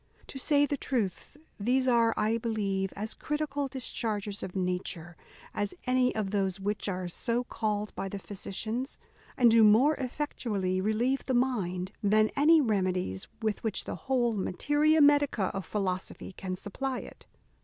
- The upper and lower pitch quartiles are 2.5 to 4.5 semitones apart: No, average, 5.0 semitones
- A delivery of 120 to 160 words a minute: Yes, average, 155 wpm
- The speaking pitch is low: No, high, 215 Hz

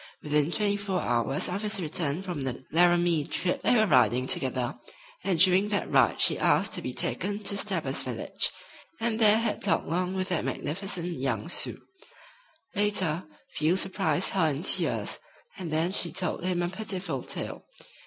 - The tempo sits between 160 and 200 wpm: Yes, average, 170 wpm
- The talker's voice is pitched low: No, medium, 180 Hz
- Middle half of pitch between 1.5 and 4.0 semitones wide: No, average, 4.5 semitones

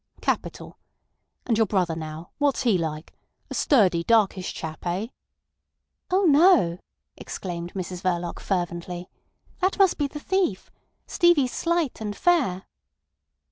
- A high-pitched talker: Yes, high, 195 Hz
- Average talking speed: No, slow, 115 wpm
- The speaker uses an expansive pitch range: Yes, wide, 9.0 semitones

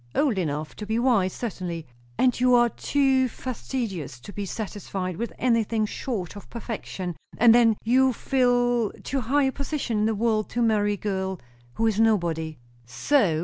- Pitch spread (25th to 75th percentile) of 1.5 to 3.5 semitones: No, average, 4.3 semitones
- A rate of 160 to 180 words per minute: Yes, average, 170 wpm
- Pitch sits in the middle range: No, high, 225 Hz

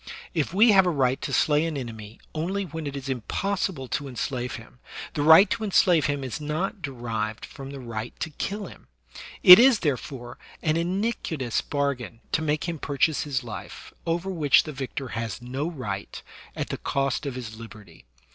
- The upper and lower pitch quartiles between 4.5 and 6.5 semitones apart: Yes, average, 5.1 semitones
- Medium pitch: Yes, medium, 145 Hz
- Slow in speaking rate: No, average, 185 wpm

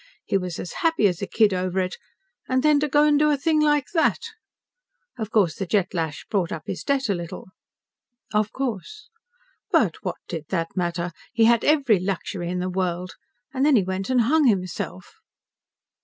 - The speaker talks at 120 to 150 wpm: No, average, 190 wpm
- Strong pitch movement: Yes, wide, 7.4 semitones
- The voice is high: Yes, high, 200 Hz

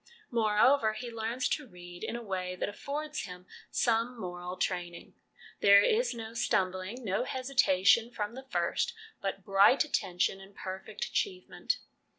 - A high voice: Yes, high, 215 Hz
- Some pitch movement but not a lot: Yes, average, 4.9 semitones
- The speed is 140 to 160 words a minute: Yes, average, 145 wpm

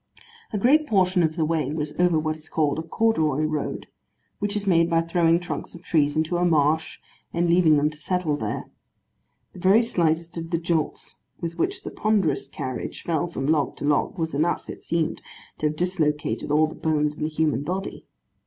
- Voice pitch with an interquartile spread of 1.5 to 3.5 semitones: Yes, narrow, 2.5 semitones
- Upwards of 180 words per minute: Yes, average, 200 wpm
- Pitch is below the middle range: No, medium, 165 Hz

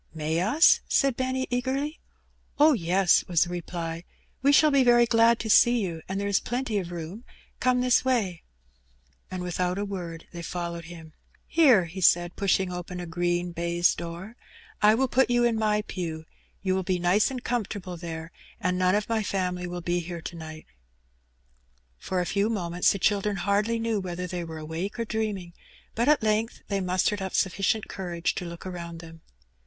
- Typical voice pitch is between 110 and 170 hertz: No, medium, 185 Hz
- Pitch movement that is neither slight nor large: Yes, average, 4.3 semitones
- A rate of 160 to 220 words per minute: Yes, average, 190 wpm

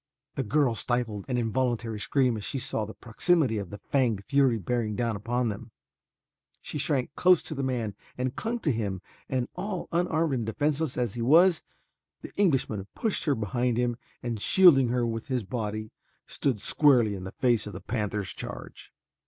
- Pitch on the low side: Yes, low, 120 Hz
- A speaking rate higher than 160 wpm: Yes, average, 180 wpm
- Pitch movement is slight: No, average, 4.1 semitones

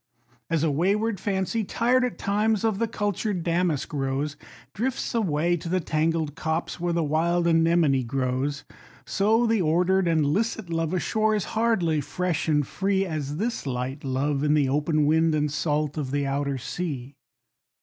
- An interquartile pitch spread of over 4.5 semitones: Yes, average, 4.9 semitones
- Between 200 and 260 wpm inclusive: No, average, 165 wpm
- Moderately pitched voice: Yes, medium, 165 Hz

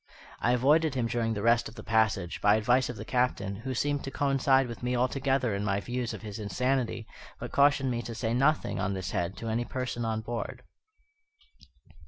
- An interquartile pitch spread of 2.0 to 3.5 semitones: Yes, average, 3.0 semitones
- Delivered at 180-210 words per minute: Yes, fast, 205 wpm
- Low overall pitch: Yes, low, 120 Hz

